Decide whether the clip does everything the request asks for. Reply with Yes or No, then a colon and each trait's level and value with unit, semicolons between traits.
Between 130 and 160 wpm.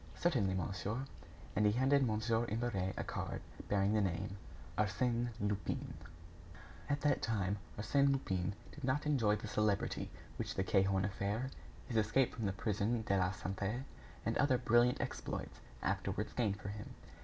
Yes: average, 155 wpm